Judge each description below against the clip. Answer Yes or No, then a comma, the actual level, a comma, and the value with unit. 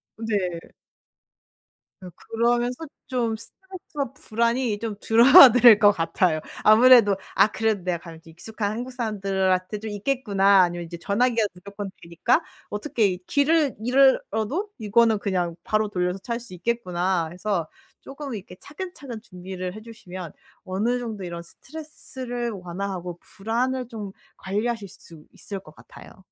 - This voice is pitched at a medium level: No, high, 215 Hz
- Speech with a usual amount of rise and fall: Yes, average, 4.6 semitones